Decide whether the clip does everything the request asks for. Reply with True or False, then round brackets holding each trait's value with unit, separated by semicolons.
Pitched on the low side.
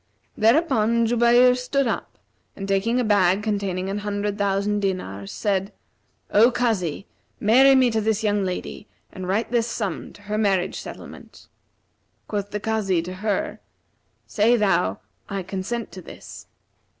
False (205 Hz)